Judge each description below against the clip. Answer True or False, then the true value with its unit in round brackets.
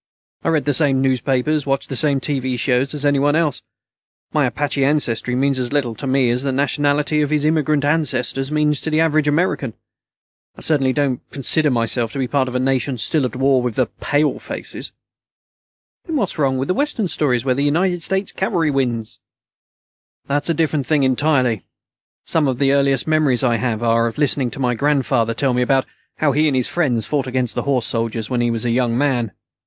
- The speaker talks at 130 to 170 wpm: False (200 wpm)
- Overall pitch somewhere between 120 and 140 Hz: True (135 Hz)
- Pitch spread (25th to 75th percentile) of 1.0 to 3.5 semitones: True (3.0 semitones)